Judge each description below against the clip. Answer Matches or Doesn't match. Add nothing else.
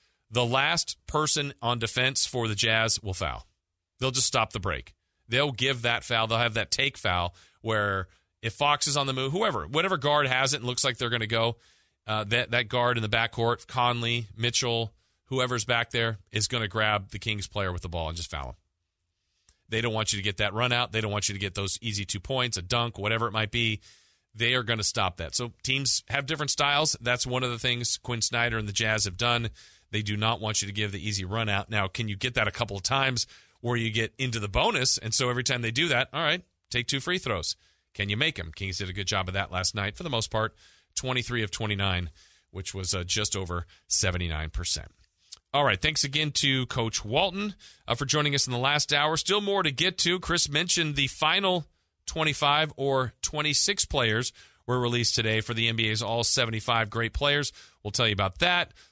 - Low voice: Matches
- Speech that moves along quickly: Matches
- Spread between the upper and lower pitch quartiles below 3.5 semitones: Doesn't match